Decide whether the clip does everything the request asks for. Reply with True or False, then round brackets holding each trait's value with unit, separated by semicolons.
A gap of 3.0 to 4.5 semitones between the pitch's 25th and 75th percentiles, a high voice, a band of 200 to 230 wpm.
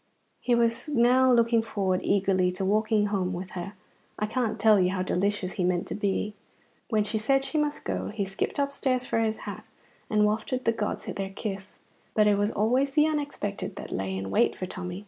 True (3.6 semitones; 210 Hz; 205 wpm)